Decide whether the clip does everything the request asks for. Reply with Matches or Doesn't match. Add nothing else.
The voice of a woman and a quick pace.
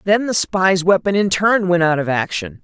Matches